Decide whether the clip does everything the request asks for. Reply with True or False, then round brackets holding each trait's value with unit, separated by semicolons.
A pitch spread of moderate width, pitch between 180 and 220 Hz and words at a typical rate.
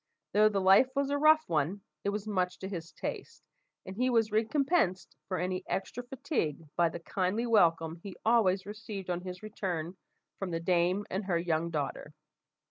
True (3.9 semitones; 190 Hz; 180 wpm)